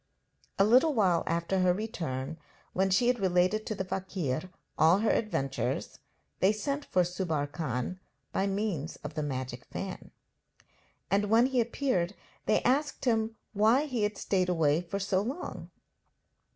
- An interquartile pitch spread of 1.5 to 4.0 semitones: No, average, 4.7 semitones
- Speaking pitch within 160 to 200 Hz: Yes, high, 190 Hz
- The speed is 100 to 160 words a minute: Yes, average, 150 wpm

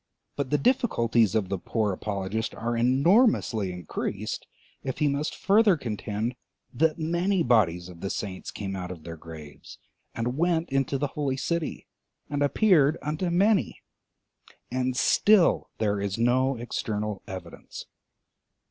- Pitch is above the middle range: No, low, 125 Hz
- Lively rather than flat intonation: Yes, wide, 7.2 semitones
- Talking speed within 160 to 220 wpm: No, average, 140 wpm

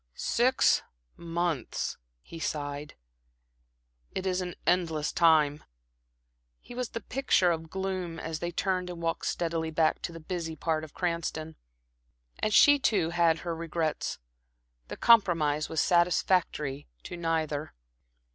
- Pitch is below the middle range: No, medium, 165 Hz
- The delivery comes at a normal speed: No, slow, 130 wpm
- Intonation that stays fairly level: Yes, narrow, 2.3 semitones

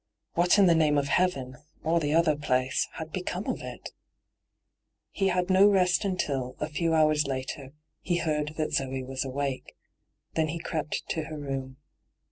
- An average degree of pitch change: Yes, average, 4.0 semitones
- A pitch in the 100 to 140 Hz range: No, medium, 155 Hz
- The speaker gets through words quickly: No, average, 170 wpm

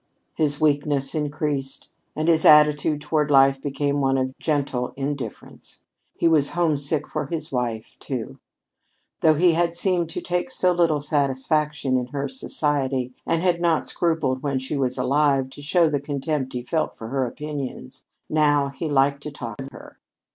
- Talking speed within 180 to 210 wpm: No, average, 165 wpm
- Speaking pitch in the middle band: Yes, medium, 145 Hz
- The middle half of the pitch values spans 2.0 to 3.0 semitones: Yes, narrow, 2.6 semitones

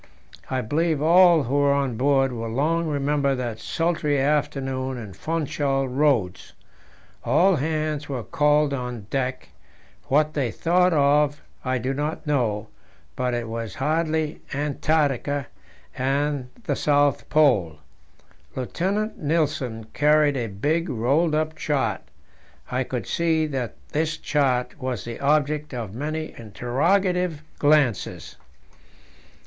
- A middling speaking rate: No, slow, 120 wpm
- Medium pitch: Yes, medium, 145 Hz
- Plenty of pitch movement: No, average, 3.3 semitones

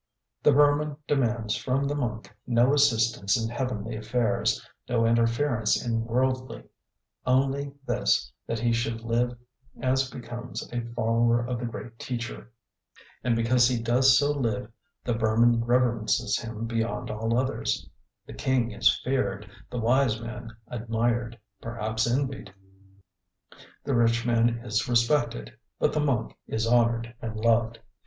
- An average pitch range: No, narrow, 1.8 semitones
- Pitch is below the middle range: Yes, low, 120 Hz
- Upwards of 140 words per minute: No, slow, 135 wpm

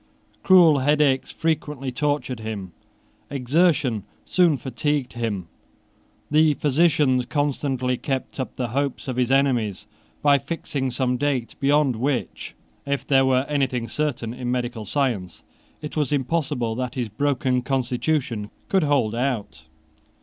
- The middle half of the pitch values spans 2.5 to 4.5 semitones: Yes, average, 3.0 semitones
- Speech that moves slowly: Yes, slow, 130 wpm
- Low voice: Yes, low, 130 Hz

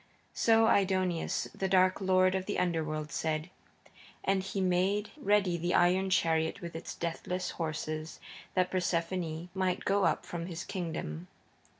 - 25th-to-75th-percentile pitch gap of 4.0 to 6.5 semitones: No, narrow, 2.4 semitones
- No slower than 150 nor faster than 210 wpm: No, average, 140 wpm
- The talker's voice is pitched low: No, medium, 180 Hz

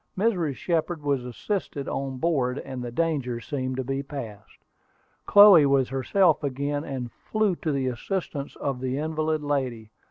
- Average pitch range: Yes, average, 3.6 semitones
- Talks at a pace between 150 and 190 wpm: Yes, average, 155 wpm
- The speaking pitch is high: No, medium, 140 Hz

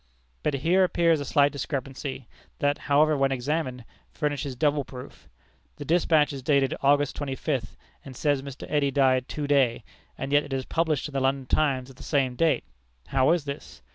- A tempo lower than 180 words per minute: No, average, 185 wpm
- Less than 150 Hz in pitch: Yes, medium, 140 Hz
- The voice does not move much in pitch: Yes, narrow, 2.1 semitones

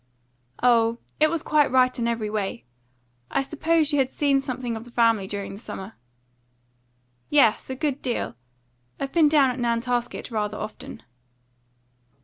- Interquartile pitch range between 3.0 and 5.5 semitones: Yes, average, 3.6 semitones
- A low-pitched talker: No, high, 245 Hz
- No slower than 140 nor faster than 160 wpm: Yes, average, 150 wpm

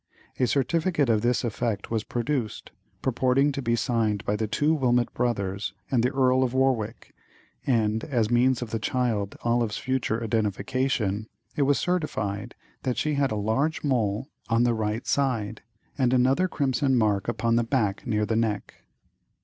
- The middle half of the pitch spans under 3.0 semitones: No, average, 3.3 semitones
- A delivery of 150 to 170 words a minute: Yes, average, 165 wpm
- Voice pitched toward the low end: Yes, low, 120 Hz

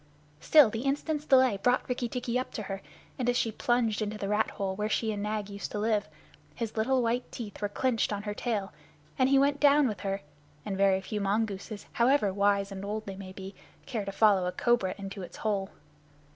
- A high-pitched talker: Yes, high, 215 Hz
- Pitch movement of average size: Yes, average, 3.6 semitones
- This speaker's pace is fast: Yes, fast, 215 wpm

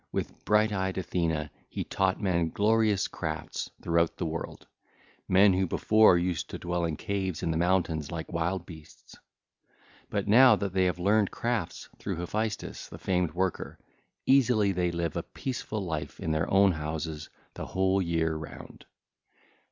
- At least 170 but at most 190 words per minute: No, average, 155 wpm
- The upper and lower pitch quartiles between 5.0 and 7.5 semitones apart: No, average, 3.3 semitones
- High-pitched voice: No, very low, 90 Hz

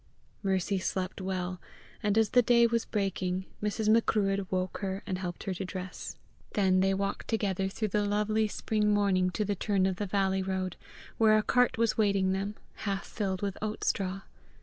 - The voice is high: Yes, high, 195 Hz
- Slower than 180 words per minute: No, average, 185 wpm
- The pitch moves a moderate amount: No, narrow, 2.0 semitones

